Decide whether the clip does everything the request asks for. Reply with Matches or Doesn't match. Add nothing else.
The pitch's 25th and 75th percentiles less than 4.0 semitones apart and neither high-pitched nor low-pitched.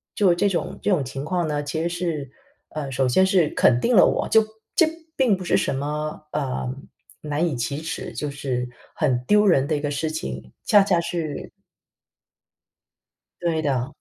Doesn't match